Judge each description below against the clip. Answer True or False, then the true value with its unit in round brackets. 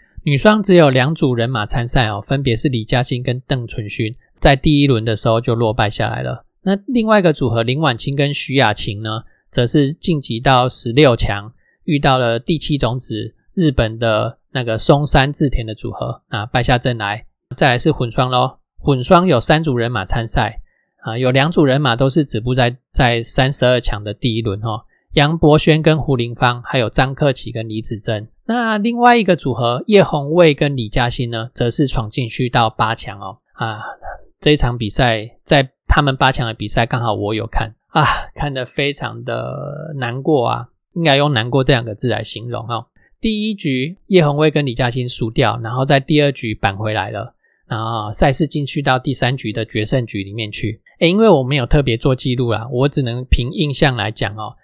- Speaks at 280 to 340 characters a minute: True (285 characters per minute)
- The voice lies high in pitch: False (130 Hz)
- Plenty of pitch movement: False (4.1 semitones)